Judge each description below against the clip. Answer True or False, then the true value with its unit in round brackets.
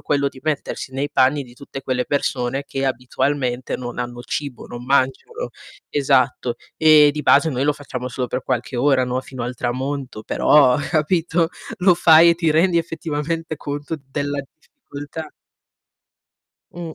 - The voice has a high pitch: False (140 Hz)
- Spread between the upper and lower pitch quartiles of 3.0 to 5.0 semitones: True (3.4 semitones)